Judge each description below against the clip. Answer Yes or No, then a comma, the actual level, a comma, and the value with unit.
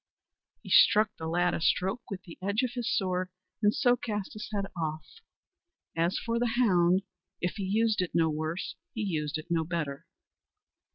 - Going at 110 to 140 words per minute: No, average, 180 wpm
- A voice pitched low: No, medium, 185 Hz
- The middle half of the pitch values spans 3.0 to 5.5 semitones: Yes, average, 4.3 semitones